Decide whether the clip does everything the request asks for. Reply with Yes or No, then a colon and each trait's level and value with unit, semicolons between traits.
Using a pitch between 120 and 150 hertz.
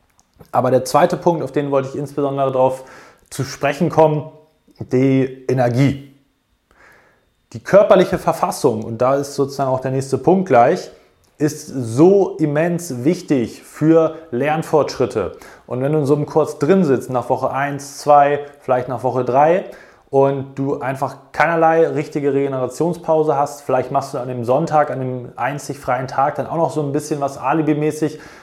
Yes: medium, 140 Hz